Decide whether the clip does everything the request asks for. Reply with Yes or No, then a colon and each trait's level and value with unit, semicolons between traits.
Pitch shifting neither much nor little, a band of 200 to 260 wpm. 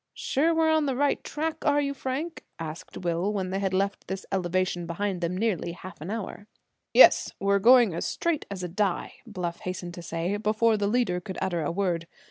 Yes: average, 5.0 semitones; fast, 205 wpm